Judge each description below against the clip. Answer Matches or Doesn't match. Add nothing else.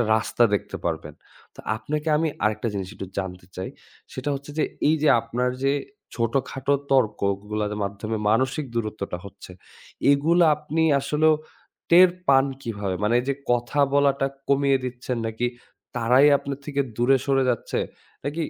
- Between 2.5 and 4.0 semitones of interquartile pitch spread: Doesn't match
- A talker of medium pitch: Doesn't match